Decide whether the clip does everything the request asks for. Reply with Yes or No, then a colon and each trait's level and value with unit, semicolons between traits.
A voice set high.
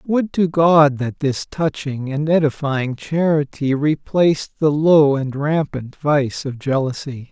No: medium, 145 Hz